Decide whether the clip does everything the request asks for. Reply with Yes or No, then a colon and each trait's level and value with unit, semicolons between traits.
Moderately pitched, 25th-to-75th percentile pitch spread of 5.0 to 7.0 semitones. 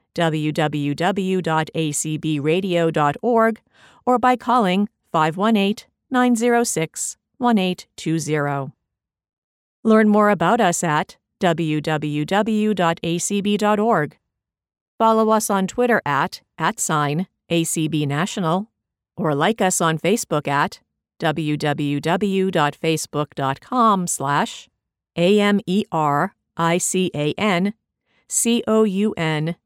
Yes: medium, 175 Hz; wide, 5.4 semitones